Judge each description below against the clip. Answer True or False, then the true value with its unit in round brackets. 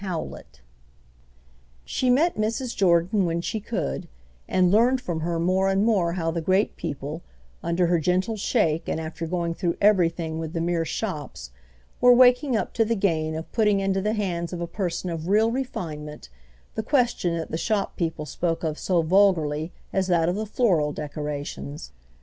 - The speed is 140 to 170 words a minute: False (180 wpm)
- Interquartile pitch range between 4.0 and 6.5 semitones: True (4.3 semitones)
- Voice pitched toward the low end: False (175 Hz)